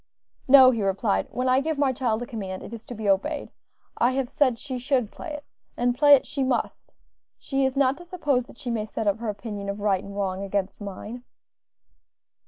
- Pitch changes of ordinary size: Yes, average, 4.8 semitones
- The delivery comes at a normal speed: No, fast, 215 wpm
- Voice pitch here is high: Yes, high, 245 Hz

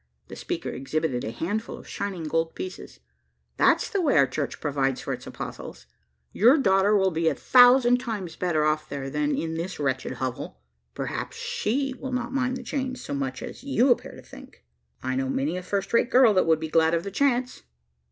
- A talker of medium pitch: Yes, medium, 180 Hz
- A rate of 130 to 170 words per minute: No, average, 200 wpm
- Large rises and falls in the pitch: Yes, wide, 8.7 semitones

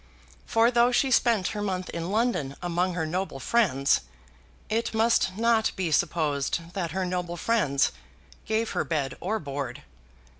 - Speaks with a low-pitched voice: No, medium, 185 Hz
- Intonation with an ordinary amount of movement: No, wide, 5.9 semitones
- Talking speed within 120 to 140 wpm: No, average, 150 wpm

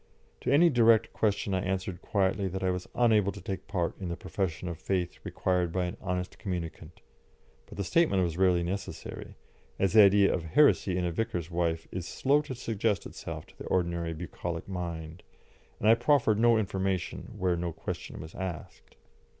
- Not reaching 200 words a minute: Yes, average, 180 wpm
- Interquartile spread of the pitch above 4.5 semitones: No, average, 3.2 semitones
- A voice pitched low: Yes, very low, 95 Hz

